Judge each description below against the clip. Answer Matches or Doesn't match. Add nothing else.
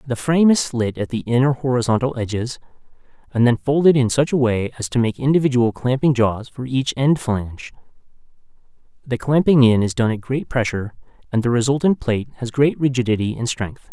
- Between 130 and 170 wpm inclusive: Doesn't match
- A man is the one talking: Matches